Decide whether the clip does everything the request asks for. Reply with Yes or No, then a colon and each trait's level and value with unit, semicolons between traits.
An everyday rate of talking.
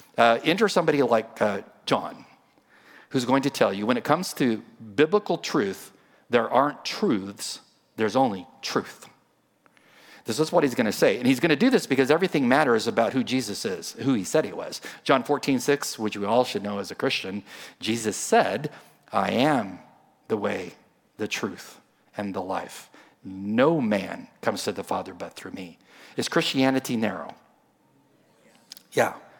Yes: average, 170 wpm